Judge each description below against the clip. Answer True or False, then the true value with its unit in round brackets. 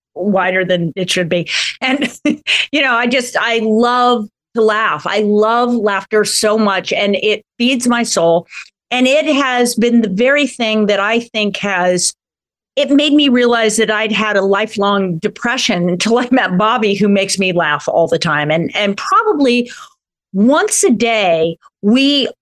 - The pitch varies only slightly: False (3.9 semitones)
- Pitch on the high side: True (215 Hz)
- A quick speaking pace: False (170 wpm)